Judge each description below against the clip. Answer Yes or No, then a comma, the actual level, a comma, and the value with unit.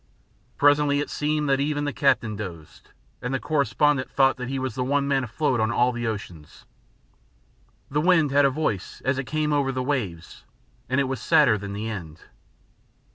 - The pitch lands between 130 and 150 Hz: Yes, low, 135 Hz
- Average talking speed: Yes, average, 185 wpm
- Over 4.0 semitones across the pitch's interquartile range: Yes, average, 4.5 semitones